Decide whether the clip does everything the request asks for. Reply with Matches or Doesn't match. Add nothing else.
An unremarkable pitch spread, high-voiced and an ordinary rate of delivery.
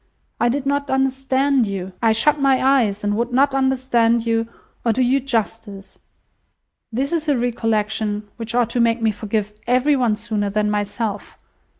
Matches